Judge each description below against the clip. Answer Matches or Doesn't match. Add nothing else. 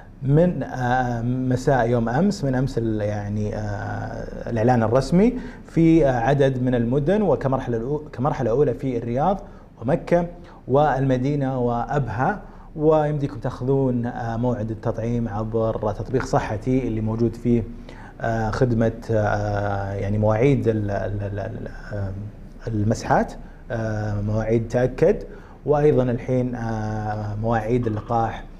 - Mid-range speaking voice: Doesn't match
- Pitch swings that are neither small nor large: Matches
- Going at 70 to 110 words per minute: Matches